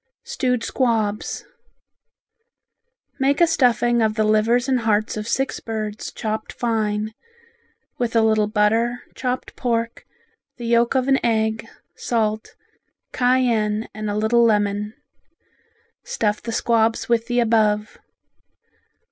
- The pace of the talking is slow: Yes, slow, 120 wpm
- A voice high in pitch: Yes, high, 225 Hz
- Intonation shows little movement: Yes, narrow, 2.0 semitones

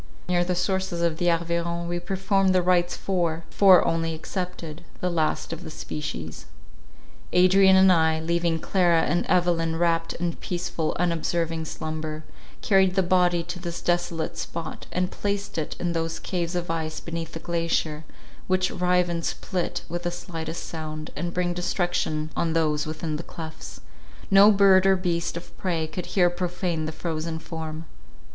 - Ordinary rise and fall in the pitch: No, narrow, 1.8 semitones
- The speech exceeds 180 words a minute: No, average, 160 wpm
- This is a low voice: No, medium, 170 Hz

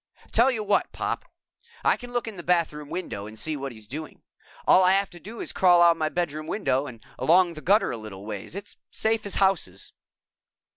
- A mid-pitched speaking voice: Yes, medium, 170 Hz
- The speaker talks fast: Yes, fast, 210 wpm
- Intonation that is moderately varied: No, wide, 6.3 semitones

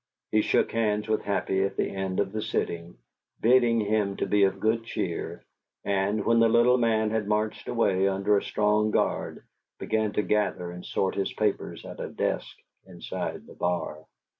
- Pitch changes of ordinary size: No, narrow, 2.1 semitones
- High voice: No, low, 105 Hz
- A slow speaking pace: No, average, 175 wpm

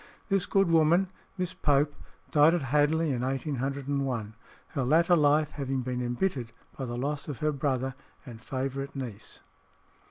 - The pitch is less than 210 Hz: Yes, medium, 140 Hz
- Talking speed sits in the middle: Yes, average, 150 wpm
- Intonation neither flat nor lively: Yes, average, 3.0 semitones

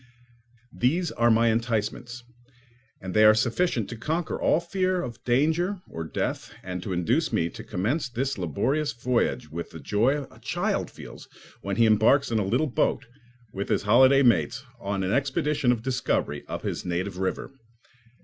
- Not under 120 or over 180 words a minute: Yes, average, 170 wpm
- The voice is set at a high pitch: No, low, 120 Hz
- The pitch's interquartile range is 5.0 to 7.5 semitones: Yes, average, 5.3 semitones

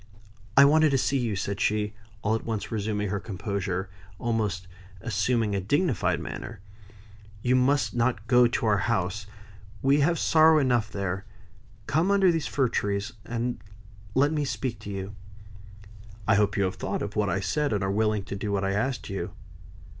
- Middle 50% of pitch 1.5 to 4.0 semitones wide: No, average, 4.6 semitones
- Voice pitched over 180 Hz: No, low, 110 Hz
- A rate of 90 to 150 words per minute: No, average, 185 wpm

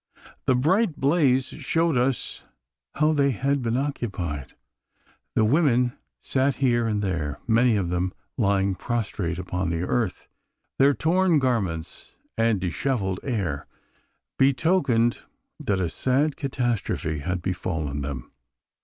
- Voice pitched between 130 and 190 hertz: No, low, 115 Hz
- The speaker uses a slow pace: Yes, slow, 120 wpm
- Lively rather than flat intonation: Yes, wide, 6.9 semitones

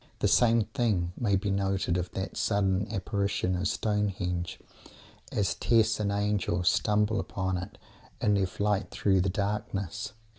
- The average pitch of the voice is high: No, low, 100 Hz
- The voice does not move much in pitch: Yes, narrow, 2.0 semitones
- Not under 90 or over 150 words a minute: Yes, average, 145 wpm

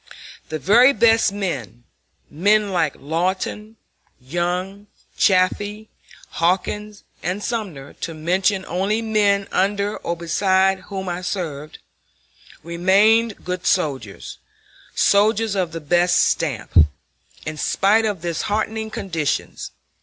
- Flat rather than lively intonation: No, average, 3.6 semitones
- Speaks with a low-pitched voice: No, high, 190 Hz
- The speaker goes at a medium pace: No, slow, 110 wpm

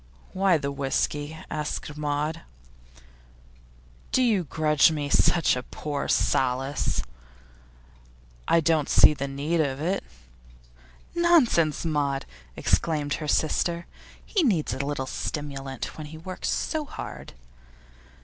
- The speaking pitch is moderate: Yes, medium, 150 Hz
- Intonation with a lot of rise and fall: No, average, 2.9 semitones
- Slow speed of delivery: Yes, slow, 110 wpm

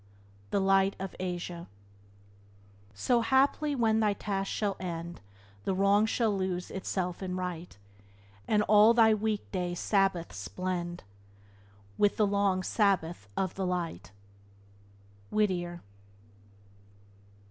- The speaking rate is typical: No, slow, 120 wpm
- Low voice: No, high, 190 Hz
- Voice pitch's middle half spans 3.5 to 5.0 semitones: No, average, 3.0 semitones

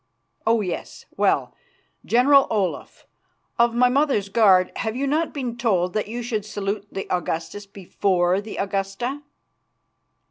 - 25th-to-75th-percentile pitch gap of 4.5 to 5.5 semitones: No, average, 3.8 semitones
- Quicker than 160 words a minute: No, slow, 135 wpm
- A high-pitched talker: Yes, high, 215 Hz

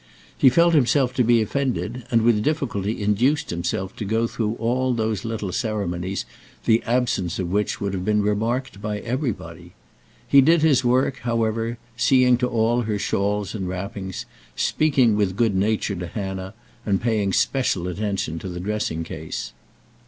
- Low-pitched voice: Yes, low, 110 Hz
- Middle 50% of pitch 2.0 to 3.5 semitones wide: No, average, 4.0 semitones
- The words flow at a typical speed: Yes, average, 160 wpm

